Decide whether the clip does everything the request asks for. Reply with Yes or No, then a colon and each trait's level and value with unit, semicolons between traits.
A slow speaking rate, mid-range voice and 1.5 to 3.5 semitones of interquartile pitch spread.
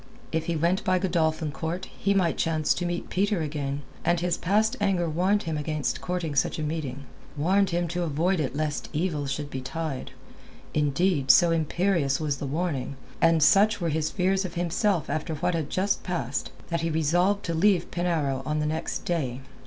No: average, 185 wpm; medium, 165 Hz; average, 3.2 semitones